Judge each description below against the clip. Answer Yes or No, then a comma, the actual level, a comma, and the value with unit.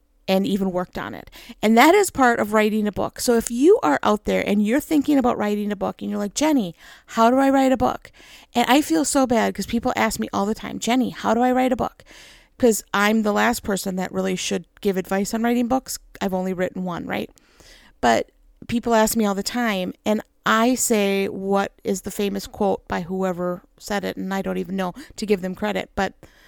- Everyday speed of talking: No, fast, 230 wpm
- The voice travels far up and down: No, average, 3.8 semitones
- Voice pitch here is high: Yes, high, 215 Hz